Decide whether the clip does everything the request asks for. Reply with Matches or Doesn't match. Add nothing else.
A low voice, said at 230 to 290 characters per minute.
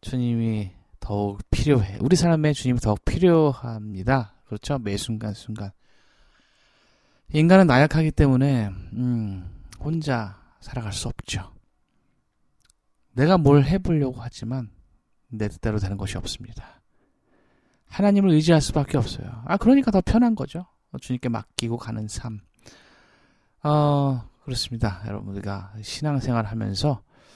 Matches